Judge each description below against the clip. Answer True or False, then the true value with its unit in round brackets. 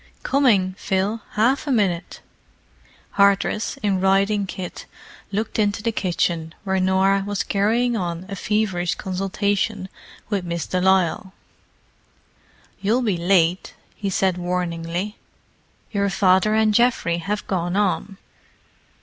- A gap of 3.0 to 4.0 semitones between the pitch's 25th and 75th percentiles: False (2.4 semitones)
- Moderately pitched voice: False (195 Hz)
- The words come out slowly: True (115 wpm)